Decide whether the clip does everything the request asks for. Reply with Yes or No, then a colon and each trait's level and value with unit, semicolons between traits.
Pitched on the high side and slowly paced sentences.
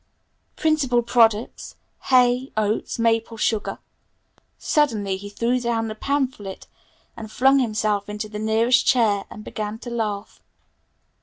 Yes: high, 225 Hz; slow, 130 wpm